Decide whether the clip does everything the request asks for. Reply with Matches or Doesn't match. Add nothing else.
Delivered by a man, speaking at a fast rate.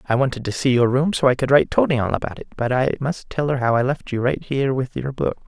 Matches